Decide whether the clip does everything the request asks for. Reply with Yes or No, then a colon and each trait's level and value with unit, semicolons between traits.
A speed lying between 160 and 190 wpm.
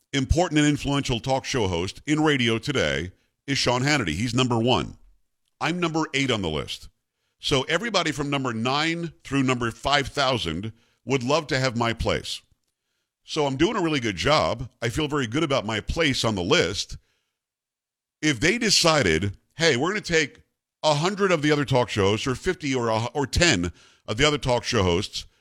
Yes: average, 185 wpm